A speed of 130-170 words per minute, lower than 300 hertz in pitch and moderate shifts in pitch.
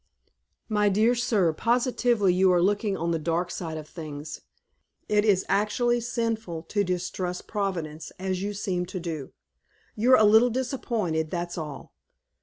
Yes: average, 150 wpm; high, 190 Hz; average, 4.5 semitones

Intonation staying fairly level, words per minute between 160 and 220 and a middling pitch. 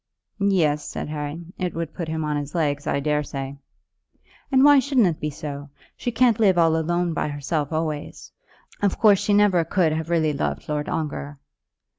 No: average, 3.9 semitones; average, 175 wpm; medium, 160 Hz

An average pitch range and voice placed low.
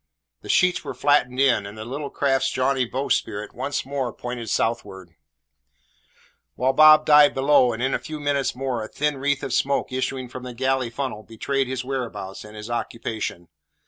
Yes: average, 3.0 semitones; low, 130 Hz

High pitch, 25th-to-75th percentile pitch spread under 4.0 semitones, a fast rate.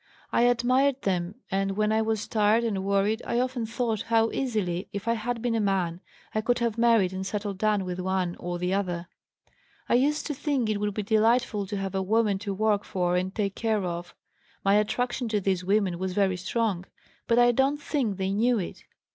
Yes: high, 210 Hz; average, 3.4 semitones; fast, 210 wpm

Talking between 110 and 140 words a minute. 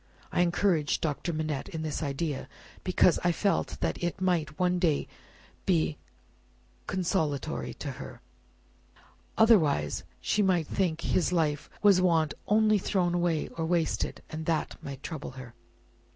Yes: slow, 135 wpm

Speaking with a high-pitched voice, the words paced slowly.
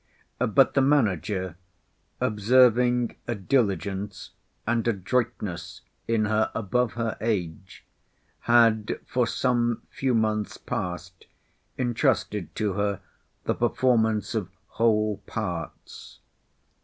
No: low, 110 Hz; slow, 95 wpm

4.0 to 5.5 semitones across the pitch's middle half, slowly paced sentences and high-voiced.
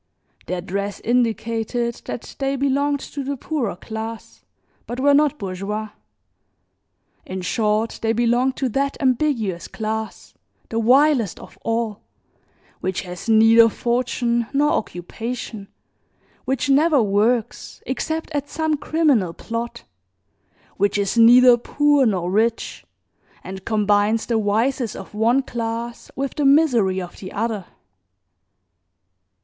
Yes: average, 4.3 semitones; slow, 120 wpm; high, 230 Hz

